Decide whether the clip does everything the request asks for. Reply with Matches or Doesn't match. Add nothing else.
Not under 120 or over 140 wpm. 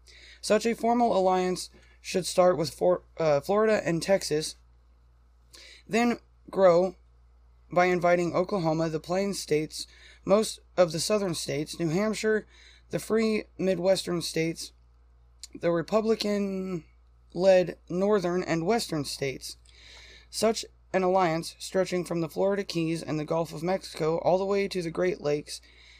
Matches